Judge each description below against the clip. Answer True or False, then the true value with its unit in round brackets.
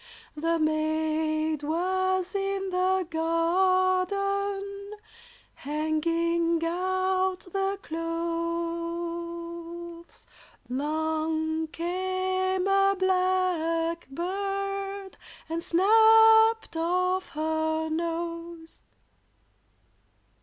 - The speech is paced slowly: True (55 wpm)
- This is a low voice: False (340 Hz)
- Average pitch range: False (2.3 semitones)